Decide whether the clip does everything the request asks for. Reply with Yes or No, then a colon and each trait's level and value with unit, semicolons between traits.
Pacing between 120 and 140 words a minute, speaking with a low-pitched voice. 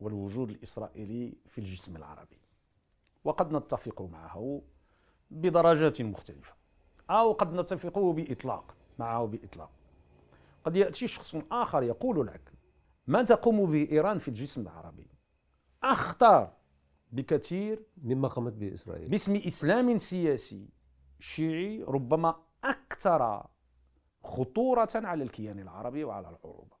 No: average, 105 wpm; low, 115 Hz